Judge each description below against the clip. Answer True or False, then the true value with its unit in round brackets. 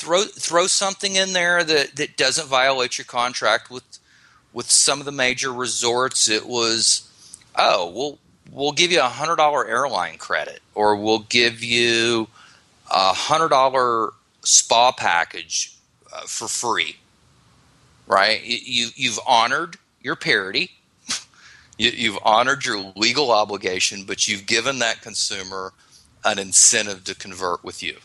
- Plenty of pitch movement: False (3.8 semitones)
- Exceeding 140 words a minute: False (135 wpm)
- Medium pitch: False (120 Hz)